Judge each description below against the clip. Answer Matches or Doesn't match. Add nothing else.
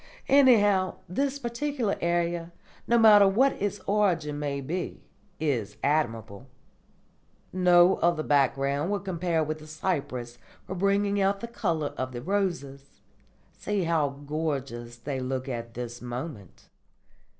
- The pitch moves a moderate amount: Doesn't match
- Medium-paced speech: Doesn't match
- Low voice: Doesn't match